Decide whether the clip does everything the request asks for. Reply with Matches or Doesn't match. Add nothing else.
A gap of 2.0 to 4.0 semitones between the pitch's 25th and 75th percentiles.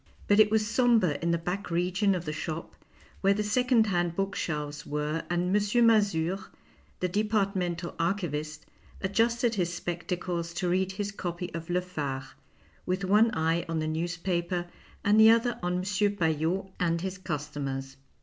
Matches